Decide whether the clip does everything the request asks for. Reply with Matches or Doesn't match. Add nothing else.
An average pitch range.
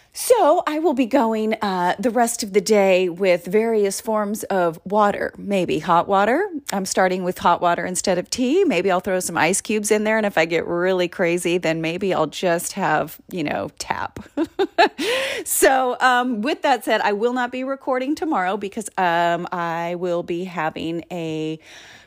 Doesn't match